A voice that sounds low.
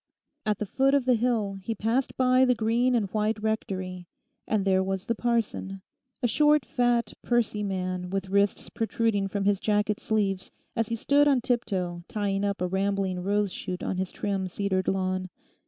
No: high, 205 Hz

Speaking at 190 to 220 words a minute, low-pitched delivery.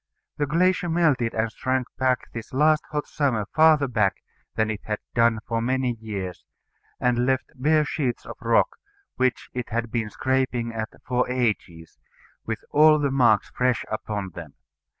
No: average, 155 wpm; low, 125 Hz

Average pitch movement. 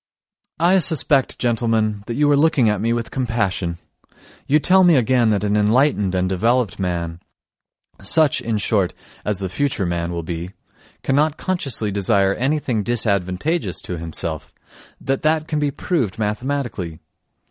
No: wide, 6.8 semitones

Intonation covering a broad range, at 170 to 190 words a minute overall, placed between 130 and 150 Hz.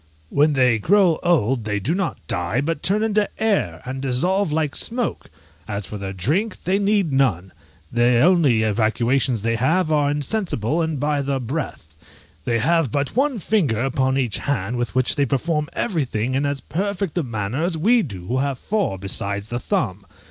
Yes: wide, 6.7 semitones; average, 180 wpm; low, 135 Hz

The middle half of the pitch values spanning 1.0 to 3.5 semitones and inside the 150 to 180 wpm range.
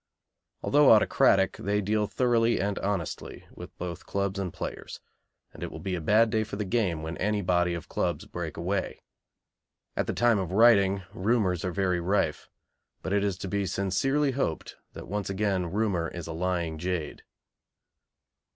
Yes: average, 2.9 semitones; average, 170 wpm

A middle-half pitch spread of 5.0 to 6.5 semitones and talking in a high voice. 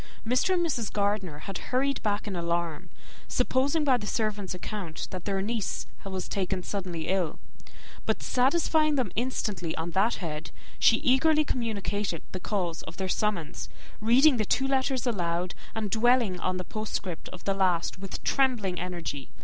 Yes: wide, 5.4 semitones; high, 205 Hz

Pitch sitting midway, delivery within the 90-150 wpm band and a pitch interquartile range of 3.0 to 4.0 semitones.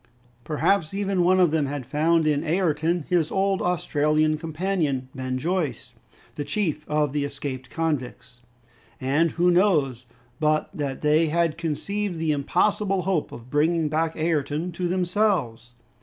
Yes: medium, 155 Hz; average, 140 wpm; average, 3.5 semitones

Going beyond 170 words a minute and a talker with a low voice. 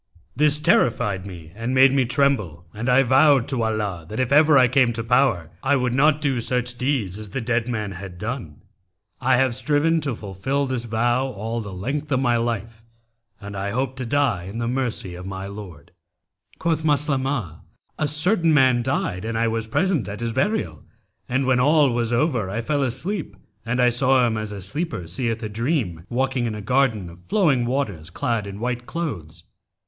Yes: average, 195 wpm; low, 120 Hz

